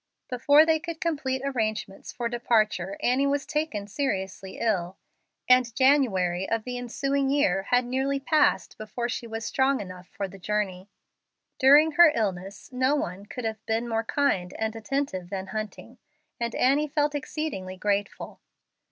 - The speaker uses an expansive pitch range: Yes, wide, 5.7 semitones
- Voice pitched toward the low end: No, high, 235 Hz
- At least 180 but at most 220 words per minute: No, average, 150 wpm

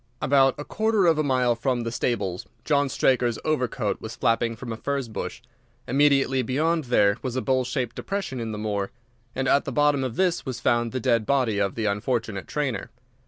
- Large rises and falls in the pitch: No, average, 3.6 semitones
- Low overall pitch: Yes, low, 125 Hz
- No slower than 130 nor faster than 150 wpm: No, average, 200 wpm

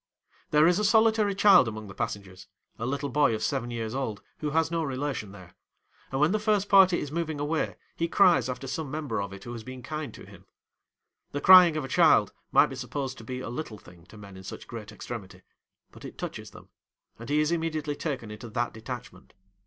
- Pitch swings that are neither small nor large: No, wide, 6.2 semitones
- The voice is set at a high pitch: No, low, 135 Hz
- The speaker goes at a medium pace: No, fast, 215 wpm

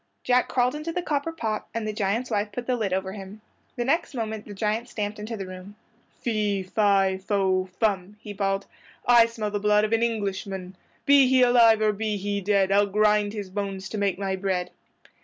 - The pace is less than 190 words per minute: No, fast, 205 wpm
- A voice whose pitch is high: Yes, high, 210 Hz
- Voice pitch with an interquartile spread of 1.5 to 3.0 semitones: Yes, average, 2.7 semitones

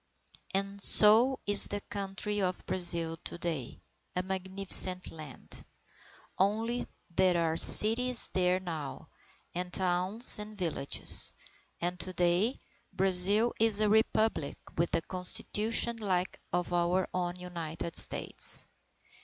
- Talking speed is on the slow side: Yes, slow, 120 wpm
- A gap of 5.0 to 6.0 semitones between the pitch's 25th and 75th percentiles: No, average, 3.1 semitones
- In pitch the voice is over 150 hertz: Yes, medium, 185 Hz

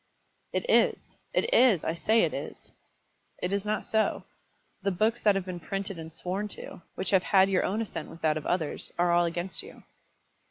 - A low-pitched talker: No, high, 190 Hz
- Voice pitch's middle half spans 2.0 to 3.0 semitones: No, average, 3.4 semitones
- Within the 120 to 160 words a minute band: No, average, 200 wpm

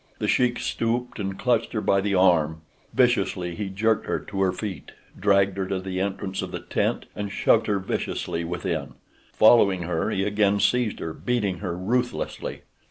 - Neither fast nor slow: Yes, average, 175 wpm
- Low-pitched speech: Yes, low, 100 Hz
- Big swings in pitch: No, average, 2.7 semitones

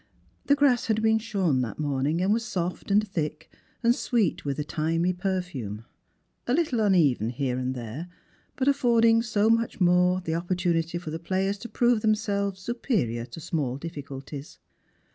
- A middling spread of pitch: No, wide, 6.8 semitones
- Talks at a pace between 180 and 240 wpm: No, average, 160 wpm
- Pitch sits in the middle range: Yes, medium, 180 Hz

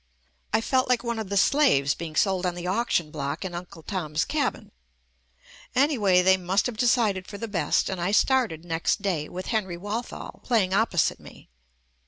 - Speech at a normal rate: Yes, average, 190 wpm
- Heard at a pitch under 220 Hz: Yes, high, 190 Hz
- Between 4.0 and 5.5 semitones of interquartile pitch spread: Yes, average, 4.6 semitones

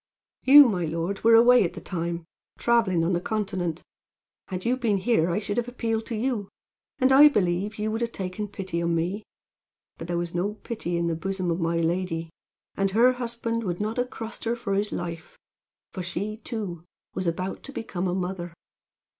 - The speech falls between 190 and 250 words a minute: Yes, average, 195 wpm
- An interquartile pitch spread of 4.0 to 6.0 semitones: Yes, average, 4.7 semitones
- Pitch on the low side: No, high, 195 Hz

